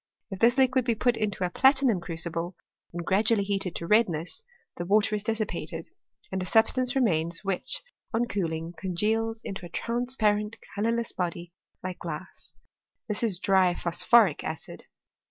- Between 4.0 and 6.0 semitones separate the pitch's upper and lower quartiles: Yes, average, 4.6 semitones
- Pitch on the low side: No, high, 200 Hz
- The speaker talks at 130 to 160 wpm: Yes, average, 155 wpm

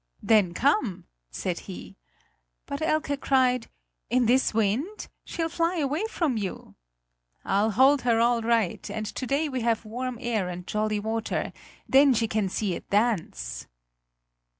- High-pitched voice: Yes, high, 235 Hz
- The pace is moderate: Yes, average, 150 wpm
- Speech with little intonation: No, average, 4.3 semitones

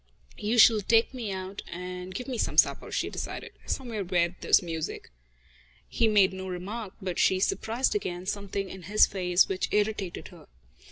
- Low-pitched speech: No, high, 195 Hz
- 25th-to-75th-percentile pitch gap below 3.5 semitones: Yes, average, 3.1 semitones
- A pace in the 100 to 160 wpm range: No, average, 170 wpm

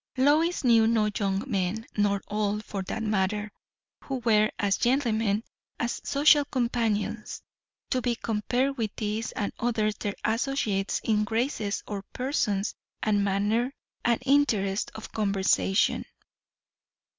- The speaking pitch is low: No, high, 220 Hz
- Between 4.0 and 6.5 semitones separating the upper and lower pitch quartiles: No, average, 3.0 semitones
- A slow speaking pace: Yes, slow, 125 wpm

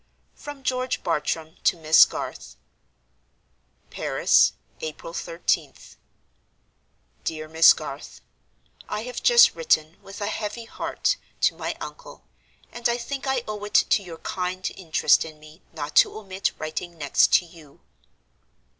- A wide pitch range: Yes, wide, 6.7 semitones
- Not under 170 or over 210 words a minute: No, slow, 135 wpm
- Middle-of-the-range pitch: Yes, medium, 180 Hz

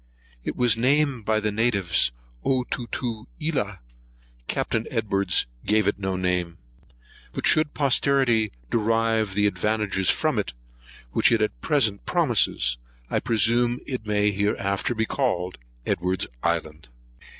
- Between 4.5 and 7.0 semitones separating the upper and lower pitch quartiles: No, average, 3.8 semitones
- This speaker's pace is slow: Yes, slow, 125 wpm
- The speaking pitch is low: Yes, low, 110 Hz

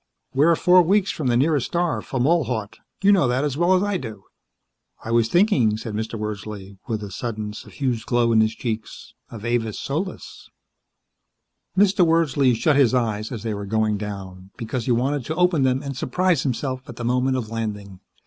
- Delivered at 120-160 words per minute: No, average, 185 wpm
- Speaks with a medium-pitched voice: No, low, 125 Hz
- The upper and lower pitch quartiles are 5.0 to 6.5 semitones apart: Yes, wide, 5.4 semitones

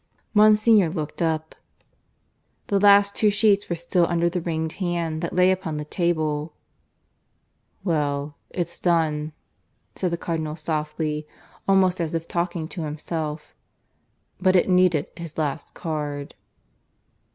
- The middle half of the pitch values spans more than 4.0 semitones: No, average, 2.9 semitones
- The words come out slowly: Yes, slow, 130 wpm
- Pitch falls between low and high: Yes, medium, 165 Hz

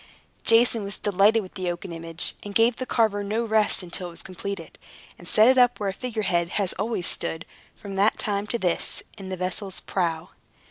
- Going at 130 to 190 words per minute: No, average, 200 wpm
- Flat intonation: No, average, 3.4 semitones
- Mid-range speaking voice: No, high, 200 Hz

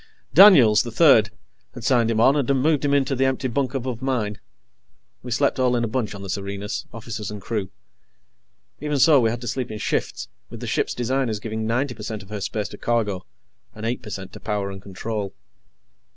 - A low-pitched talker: Yes, low, 115 Hz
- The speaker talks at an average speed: No, fast, 215 wpm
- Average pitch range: Yes, average, 3.8 semitones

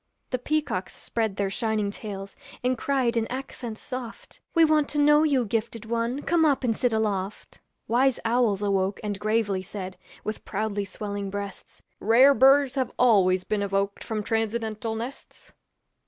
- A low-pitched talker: No, high, 225 Hz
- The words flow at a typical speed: Yes, average, 155 wpm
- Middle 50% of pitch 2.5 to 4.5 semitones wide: Yes, average, 4.0 semitones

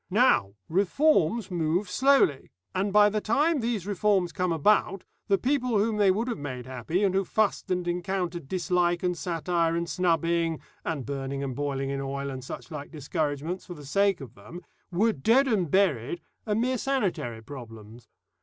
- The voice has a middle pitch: Yes, medium, 175 Hz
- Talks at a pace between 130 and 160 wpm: No, average, 170 wpm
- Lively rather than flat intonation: Yes, wide, 6.2 semitones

